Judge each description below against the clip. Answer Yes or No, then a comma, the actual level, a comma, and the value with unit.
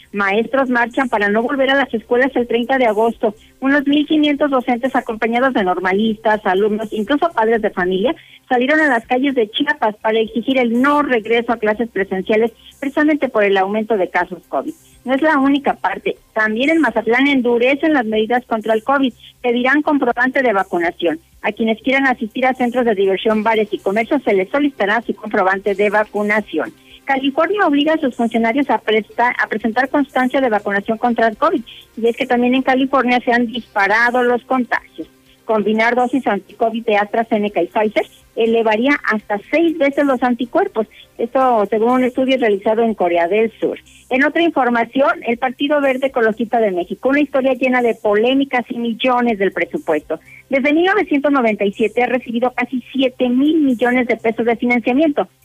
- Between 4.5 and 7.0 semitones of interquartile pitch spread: No, average, 3.6 semitones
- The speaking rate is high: No, average, 170 wpm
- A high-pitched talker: Yes, high, 240 Hz